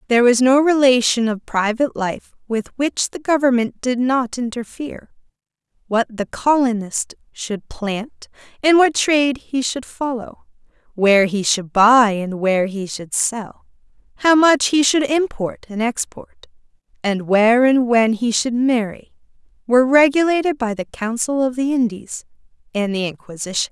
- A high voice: Yes, high, 240 Hz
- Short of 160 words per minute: Yes, average, 150 wpm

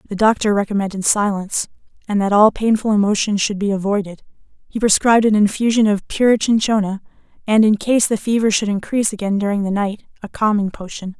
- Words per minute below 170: No, average, 175 wpm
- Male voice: No, female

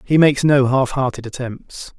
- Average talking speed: Yes, average, 180 wpm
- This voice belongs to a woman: No, male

